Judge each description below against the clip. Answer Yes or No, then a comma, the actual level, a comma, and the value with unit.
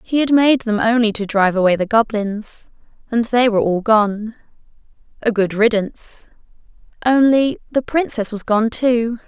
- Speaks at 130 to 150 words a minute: Yes, average, 140 wpm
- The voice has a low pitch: No, high, 225 Hz